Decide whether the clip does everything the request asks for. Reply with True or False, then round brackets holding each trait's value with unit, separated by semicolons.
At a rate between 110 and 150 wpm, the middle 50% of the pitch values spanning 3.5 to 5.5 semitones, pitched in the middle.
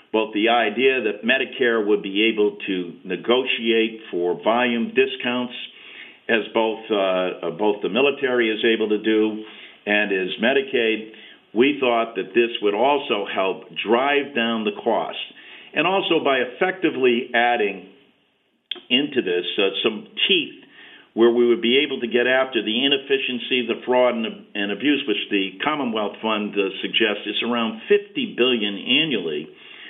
False (145 wpm; 4.0 semitones; 120 Hz)